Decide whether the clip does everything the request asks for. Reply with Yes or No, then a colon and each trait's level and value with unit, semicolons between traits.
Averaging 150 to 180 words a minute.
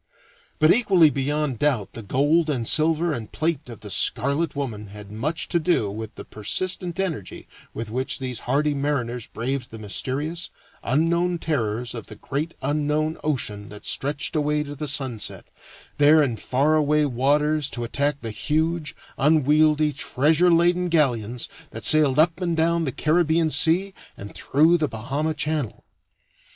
Yes: average, 155 wpm